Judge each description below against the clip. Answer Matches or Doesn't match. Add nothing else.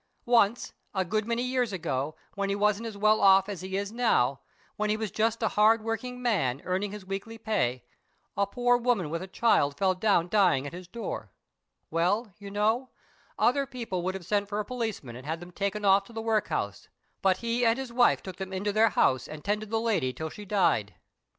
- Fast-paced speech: Matches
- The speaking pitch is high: Matches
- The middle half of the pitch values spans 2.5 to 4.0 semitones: Matches